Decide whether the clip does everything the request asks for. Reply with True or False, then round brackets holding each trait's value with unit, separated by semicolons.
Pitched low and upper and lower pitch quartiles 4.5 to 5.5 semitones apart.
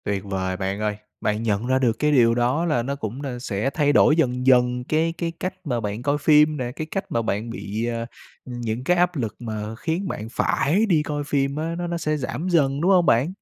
True (130 Hz; 5.1 semitones)